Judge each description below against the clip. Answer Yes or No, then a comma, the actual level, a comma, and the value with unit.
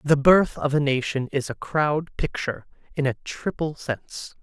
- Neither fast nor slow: Yes, average, 175 wpm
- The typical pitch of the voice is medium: Yes, medium, 145 Hz